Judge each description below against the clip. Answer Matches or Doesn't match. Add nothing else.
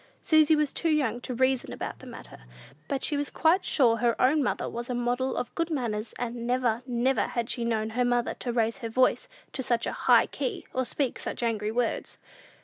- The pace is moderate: Doesn't match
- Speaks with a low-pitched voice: Doesn't match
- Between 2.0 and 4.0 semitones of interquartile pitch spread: Matches